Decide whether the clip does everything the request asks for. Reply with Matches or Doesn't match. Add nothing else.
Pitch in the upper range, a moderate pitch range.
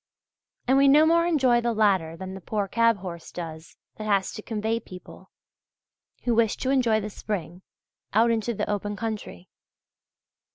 Matches